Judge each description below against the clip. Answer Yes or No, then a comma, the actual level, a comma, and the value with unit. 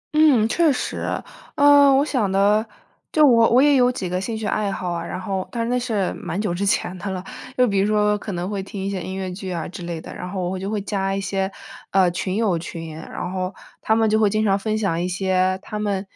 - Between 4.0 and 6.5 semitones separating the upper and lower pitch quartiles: No, average, 2.9 semitones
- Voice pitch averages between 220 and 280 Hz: No, high, 195 Hz